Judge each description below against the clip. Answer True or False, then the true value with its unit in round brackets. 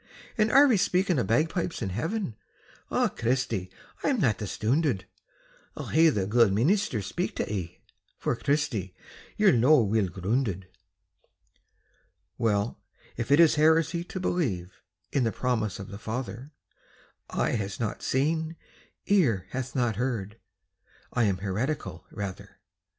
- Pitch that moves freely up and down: True (7.6 semitones)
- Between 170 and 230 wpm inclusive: False (135 wpm)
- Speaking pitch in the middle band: False (120 Hz)